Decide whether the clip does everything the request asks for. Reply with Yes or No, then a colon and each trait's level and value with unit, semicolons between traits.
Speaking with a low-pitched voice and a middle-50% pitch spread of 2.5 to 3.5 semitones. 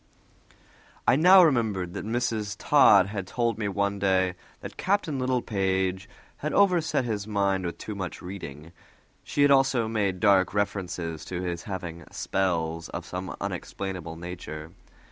No: low, 100 Hz; average, 4.4 semitones